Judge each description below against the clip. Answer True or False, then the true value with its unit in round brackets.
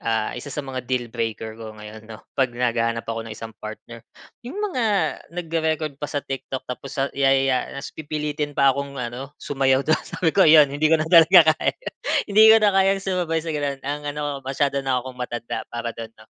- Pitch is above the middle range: False (140 Hz)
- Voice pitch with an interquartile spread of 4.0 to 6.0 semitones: True (4.4 semitones)